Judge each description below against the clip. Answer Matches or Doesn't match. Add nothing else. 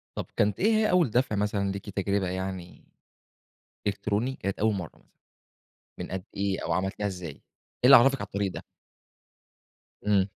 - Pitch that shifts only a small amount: Matches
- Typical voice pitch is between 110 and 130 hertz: Doesn't match